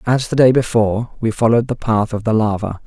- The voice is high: No, low, 115 Hz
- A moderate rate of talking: No, fast, 230 wpm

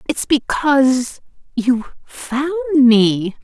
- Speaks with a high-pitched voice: Yes, very high, 260 Hz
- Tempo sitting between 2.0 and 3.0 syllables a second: Yes, 2.9 syllables/s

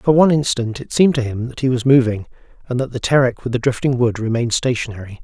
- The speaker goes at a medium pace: No, fast, 240 wpm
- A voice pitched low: Yes, low, 125 Hz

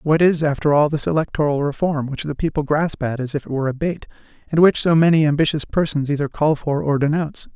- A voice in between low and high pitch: Yes, medium, 150 Hz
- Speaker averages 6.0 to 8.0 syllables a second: Yes, 6.1 syllables/s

